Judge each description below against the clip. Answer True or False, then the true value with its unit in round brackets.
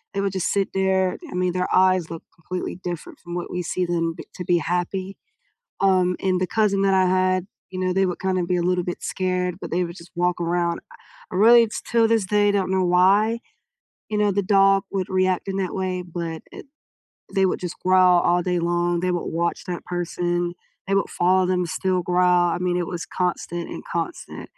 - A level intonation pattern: True (1.5 semitones)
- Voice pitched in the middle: True (180 Hz)